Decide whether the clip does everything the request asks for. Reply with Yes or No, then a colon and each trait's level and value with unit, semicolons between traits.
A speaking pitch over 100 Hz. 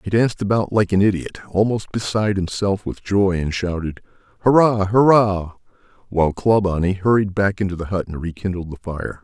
No: very low, 95 Hz